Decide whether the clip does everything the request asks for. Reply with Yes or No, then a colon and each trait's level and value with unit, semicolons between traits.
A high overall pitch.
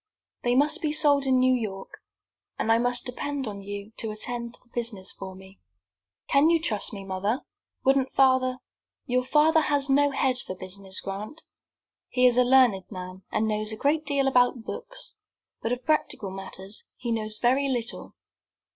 Yes: high, 245 Hz